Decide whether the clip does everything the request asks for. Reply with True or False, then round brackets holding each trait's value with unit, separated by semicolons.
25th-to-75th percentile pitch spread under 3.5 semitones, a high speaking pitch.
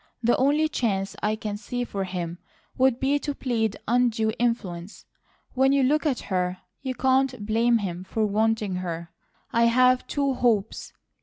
False (4.5 semitones; 230 Hz)